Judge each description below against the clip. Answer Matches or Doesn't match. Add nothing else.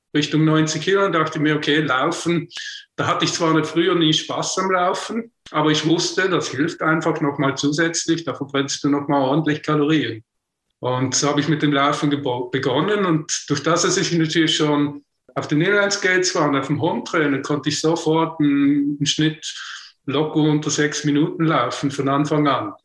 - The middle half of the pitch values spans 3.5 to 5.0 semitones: Doesn't match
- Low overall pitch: Doesn't match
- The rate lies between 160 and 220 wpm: Matches